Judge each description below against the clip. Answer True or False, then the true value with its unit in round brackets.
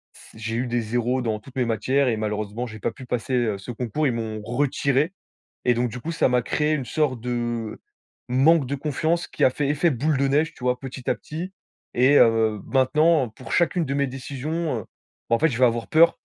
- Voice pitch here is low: True (125 Hz)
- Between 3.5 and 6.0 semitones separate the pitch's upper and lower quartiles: True (3.8 semitones)